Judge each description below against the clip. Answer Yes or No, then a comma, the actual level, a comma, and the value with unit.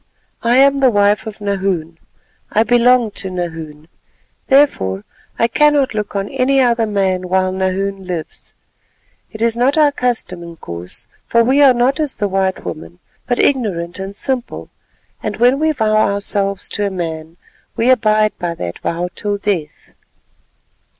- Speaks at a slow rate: No, average, 150 wpm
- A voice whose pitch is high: Yes, high, 205 Hz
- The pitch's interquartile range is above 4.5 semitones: Yes, average, 5.2 semitones